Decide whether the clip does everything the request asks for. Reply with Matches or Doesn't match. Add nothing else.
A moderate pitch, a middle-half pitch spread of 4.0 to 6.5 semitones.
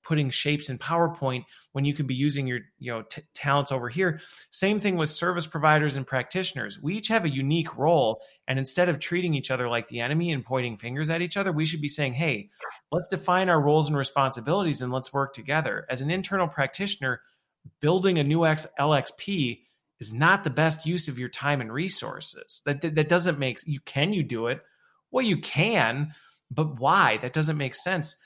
Matches